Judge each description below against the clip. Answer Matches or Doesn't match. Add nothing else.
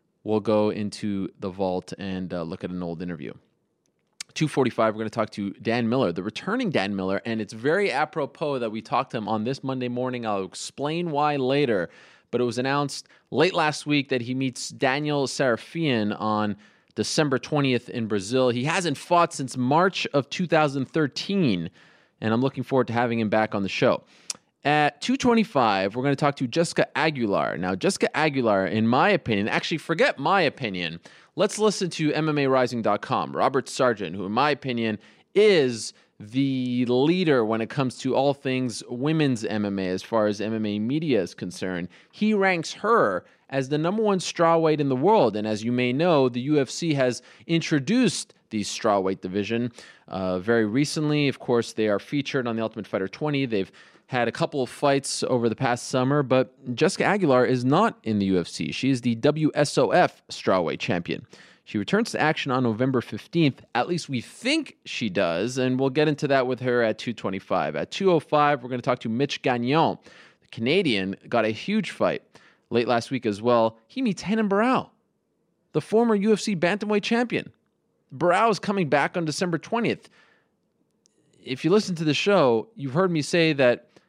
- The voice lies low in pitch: Matches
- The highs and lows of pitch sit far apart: Matches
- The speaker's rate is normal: Matches